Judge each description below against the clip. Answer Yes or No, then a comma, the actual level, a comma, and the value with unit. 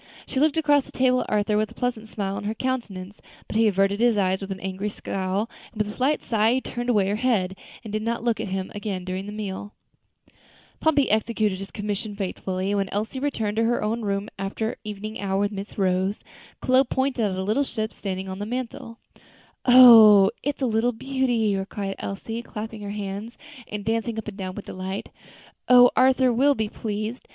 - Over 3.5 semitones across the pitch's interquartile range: No, average, 3.2 semitones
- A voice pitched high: Yes, high, 215 Hz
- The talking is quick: Yes, fast, 210 wpm